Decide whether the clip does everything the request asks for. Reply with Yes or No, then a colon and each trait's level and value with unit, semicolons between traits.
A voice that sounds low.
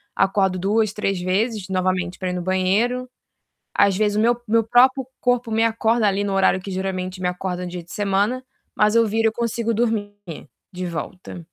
No: high, 205 Hz